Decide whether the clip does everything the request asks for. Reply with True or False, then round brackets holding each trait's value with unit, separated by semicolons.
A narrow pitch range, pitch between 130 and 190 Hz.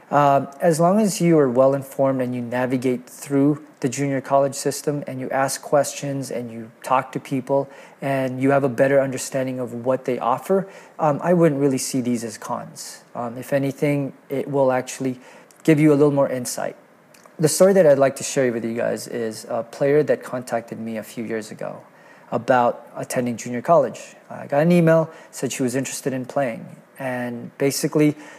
True (2.2 semitones; 135 Hz)